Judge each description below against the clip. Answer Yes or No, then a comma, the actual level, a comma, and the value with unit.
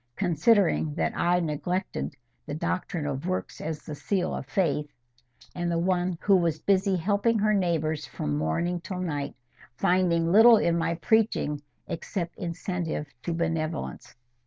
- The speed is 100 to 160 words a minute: Yes, average, 145 wpm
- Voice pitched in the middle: Yes, medium, 170 Hz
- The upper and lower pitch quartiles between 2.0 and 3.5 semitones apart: Yes, average, 3.0 semitones